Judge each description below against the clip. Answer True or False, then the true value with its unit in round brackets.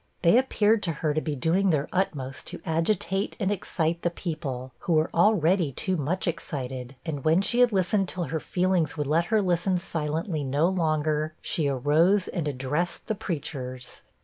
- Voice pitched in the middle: True (165 Hz)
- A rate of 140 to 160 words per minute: False (175 wpm)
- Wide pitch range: False (4.0 semitones)